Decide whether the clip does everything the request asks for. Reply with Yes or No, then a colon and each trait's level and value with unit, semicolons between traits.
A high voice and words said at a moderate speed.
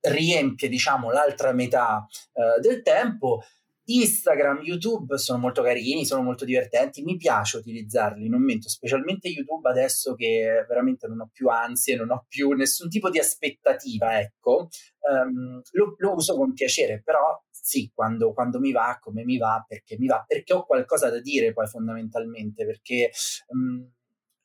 No: low, 135 Hz; average, 155 wpm